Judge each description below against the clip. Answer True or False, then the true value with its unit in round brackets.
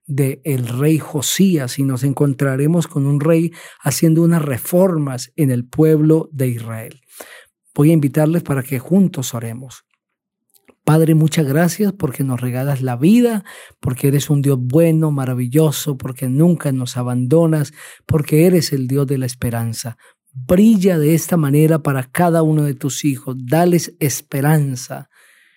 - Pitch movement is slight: False (3.4 semitones)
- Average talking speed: True (145 wpm)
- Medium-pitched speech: True (145 Hz)